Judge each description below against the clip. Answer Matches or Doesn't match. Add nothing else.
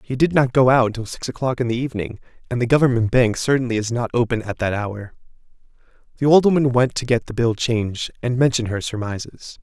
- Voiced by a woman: Doesn't match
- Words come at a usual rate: Doesn't match